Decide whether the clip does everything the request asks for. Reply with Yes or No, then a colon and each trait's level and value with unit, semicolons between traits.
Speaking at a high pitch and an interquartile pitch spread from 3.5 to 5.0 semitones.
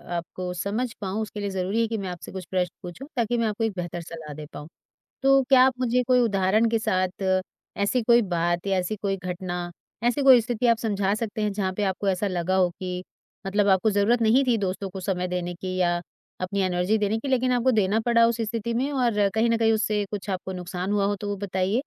Yes: high, 200 Hz; average, 3.8 semitones